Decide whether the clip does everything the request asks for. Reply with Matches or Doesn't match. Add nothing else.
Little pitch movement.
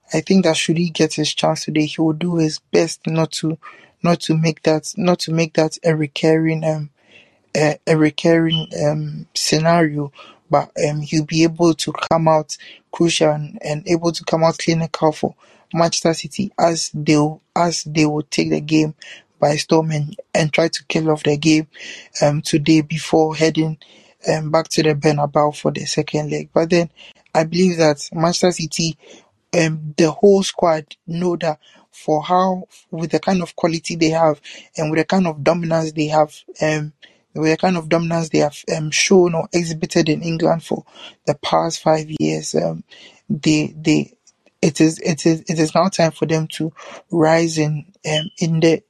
Matches